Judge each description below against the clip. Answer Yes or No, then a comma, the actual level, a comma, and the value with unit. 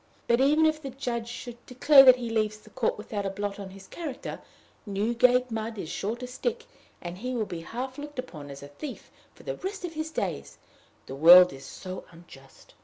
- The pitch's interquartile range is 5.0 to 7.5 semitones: Yes, wide, 5.4 semitones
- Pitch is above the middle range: Yes, high, 235 Hz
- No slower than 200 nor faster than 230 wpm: Yes, fast, 205 wpm